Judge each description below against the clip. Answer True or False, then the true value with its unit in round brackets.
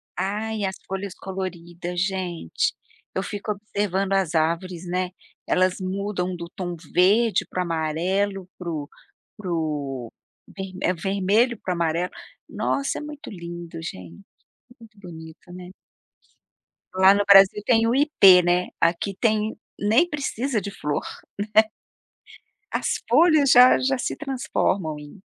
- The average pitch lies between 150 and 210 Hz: True (190 Hz)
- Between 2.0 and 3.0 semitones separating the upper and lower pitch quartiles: False (3.5 semitones)